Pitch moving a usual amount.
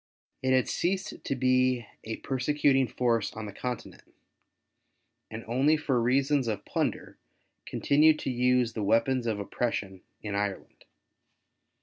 Yes: average, 3.1 semitones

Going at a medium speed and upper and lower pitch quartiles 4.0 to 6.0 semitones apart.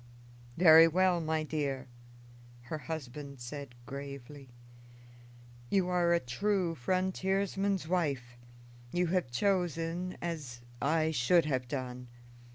No: slow, 105 wpm; average, 4.6 semitones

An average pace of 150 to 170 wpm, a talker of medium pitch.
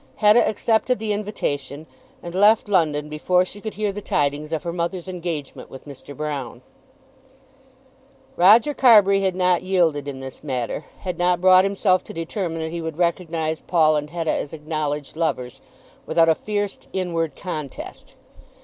Yes: average, 160 wpm; medium, 170 Hz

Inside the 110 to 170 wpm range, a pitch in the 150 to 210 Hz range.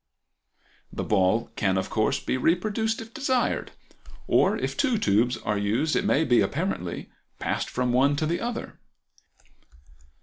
No: average, 145 wpm; medium, 140 Hz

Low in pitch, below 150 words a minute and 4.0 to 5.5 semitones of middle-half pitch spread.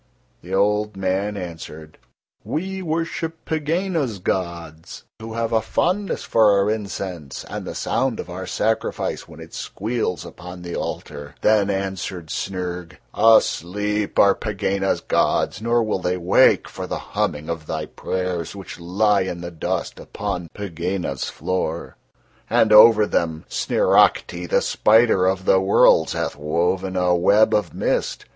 No: very low, 95 Hz; average, 140 wpm; average, 3.6 semitones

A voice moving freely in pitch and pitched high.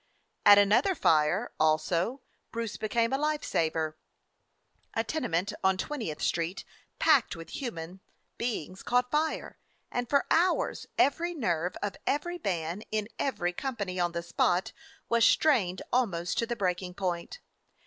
Yes: wide, 6.2 semitones; high, 205 Hz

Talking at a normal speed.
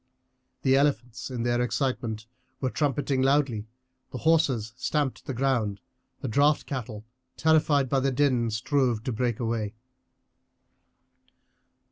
No: slow, 120 wpm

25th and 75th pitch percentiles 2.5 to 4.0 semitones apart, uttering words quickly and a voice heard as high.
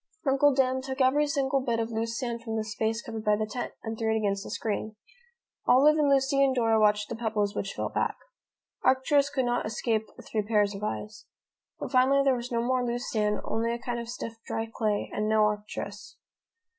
Yes: average, 3.3 semitones; fast, 210 wpm; high, 230 Hz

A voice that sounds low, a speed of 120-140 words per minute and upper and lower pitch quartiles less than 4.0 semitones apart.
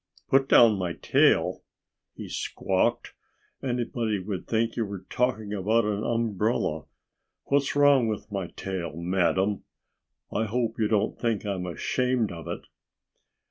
Yes: low, 105 Hz; slow, 135 wpm; average, 3.6 semitones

